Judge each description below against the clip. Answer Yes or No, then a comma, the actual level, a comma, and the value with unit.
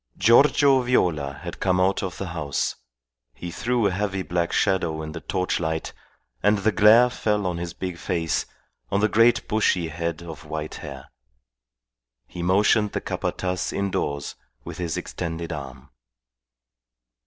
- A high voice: No, very low, 90 Hz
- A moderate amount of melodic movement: Yes, average, 4.0 semitones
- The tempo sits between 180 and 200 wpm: No, average, 145 wpm